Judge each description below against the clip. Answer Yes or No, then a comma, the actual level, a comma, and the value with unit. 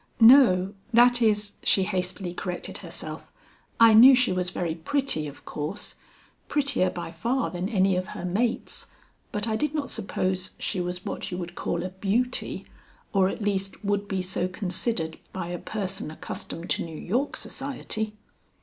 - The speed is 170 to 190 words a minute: No, average, 160 wpm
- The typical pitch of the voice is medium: No, high, 195 Hz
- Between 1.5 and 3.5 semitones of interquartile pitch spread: No, average, 4.1 semitones